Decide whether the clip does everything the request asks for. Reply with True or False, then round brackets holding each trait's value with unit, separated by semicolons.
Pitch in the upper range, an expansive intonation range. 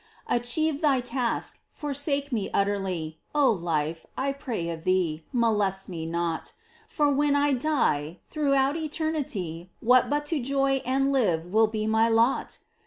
True (240 Hz; 7.4 semitones)